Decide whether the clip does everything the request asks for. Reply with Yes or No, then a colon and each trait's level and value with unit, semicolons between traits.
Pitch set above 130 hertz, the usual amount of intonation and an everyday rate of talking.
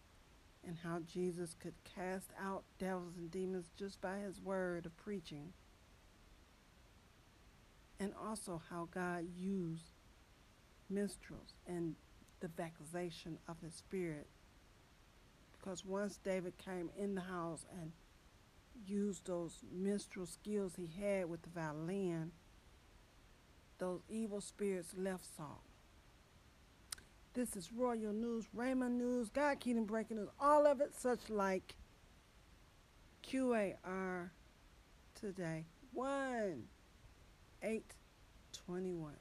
No: medium, 185 Hz; average, 3.2 semitones; slow, 105 wpm